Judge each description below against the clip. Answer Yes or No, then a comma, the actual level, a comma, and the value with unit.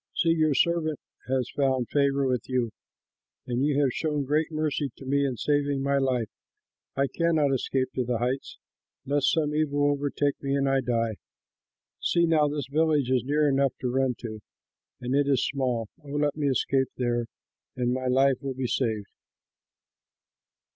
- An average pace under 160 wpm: No, average, 170 wpm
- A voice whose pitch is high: No, medium, 140 Hz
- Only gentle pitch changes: Yes, narrow, 2.3 semitones